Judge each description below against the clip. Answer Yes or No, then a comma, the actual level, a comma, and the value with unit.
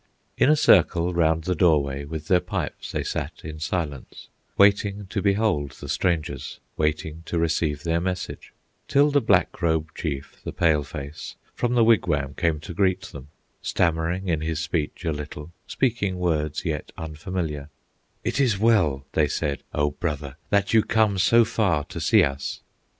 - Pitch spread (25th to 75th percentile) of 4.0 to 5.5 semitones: Yes, average, 4.4 semitones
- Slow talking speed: No, average, 165 wpm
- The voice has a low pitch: Yes, very low, 80 Hz